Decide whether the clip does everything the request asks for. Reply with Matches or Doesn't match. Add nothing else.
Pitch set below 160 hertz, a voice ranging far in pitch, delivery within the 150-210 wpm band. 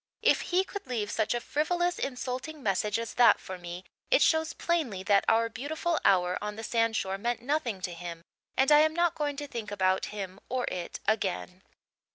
Doesn't match